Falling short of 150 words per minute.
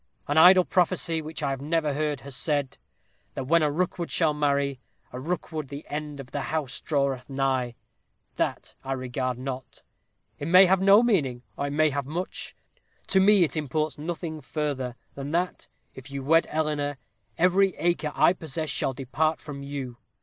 No: average, 170 wpm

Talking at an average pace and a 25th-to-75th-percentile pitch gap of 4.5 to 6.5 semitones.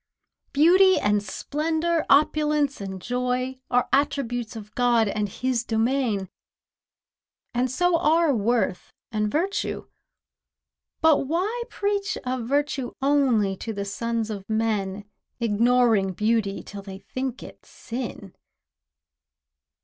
No: slow, 110 wpm; wide, 5.4 semitones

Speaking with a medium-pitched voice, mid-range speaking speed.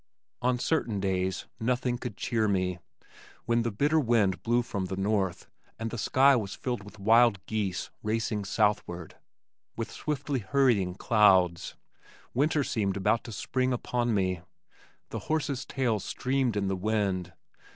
No: low, 110 Hz; average, 145 wpm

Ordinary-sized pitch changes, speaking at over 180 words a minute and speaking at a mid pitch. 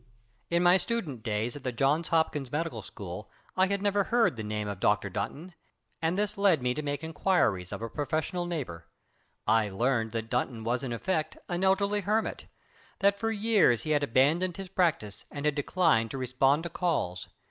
No: wide, 7.8 semitones; average, 190 wpm; medium, 150 Hz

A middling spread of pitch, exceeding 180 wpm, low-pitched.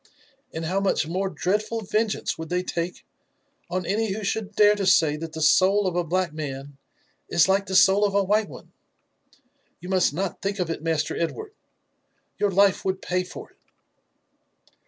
No: average, 3.1 semitones; average, 190 wpm; medium, 185 Hz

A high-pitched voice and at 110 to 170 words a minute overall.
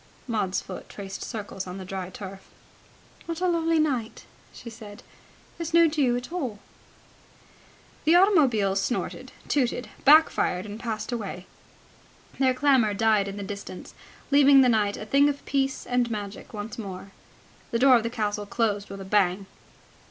Yes: high, 225 Hz; average, 160 wpm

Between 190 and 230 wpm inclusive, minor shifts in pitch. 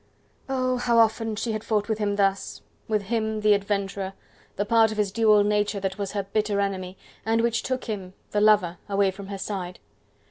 Yes: average, 200 wpm; narrow, 1.8 semitones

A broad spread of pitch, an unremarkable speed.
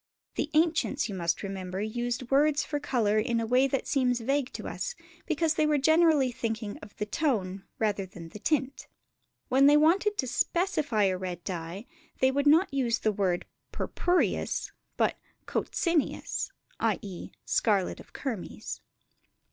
Yes: wide, 6.4 semitones; average, 155 wpm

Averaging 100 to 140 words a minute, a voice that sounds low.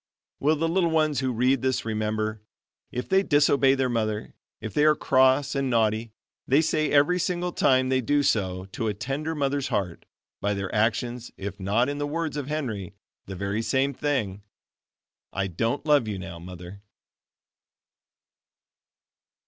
No: average, 160 wpm; low, 130 Hz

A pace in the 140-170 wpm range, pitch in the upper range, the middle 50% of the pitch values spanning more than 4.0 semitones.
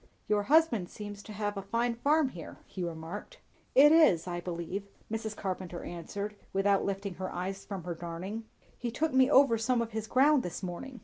No: average, 190 wpm; high, 205 Hz; average, 4.9 semitones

